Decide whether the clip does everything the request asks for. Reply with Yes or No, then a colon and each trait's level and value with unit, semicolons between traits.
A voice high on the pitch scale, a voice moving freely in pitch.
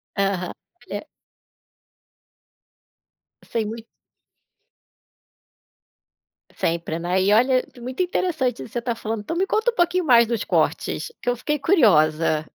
Yes: high, 235 Hz; wide, 7.4 semitones